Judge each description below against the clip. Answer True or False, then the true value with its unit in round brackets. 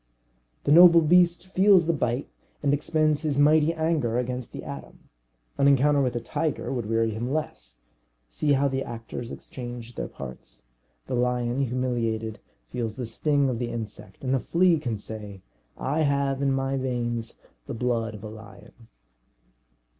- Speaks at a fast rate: False (160 wpm)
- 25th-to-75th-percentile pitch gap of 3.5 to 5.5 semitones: True (4.3 semitones)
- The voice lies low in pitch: True (125 Hz)